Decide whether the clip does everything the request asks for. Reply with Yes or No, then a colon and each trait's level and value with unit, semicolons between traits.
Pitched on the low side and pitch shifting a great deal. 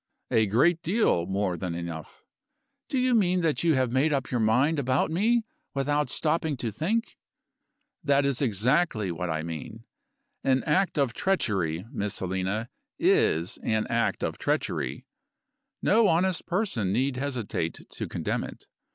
Yes: low, 130 Hz; wide, 8.3 semitones